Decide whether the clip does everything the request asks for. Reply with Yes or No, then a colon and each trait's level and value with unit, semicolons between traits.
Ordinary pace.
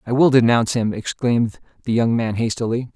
Yes: average, 185 wpm